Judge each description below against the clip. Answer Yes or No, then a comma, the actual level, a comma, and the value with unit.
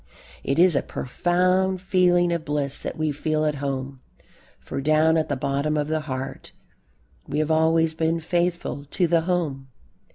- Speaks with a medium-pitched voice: Yes, medium, 155 Hz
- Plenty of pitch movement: No, average, 3.4 semitones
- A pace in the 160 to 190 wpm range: Yes, average, 165 wpm